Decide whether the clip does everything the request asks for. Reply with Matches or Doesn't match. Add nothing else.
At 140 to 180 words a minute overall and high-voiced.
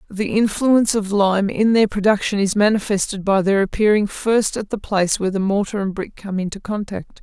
Doesn't match